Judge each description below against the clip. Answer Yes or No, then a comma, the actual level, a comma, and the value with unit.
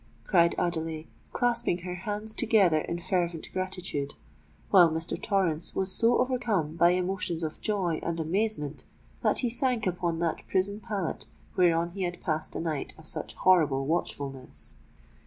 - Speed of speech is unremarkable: Yes, average, 150 wpm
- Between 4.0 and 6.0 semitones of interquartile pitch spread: No, average, 3.4 semitones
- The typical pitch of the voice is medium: Yes, medium, 175 Hz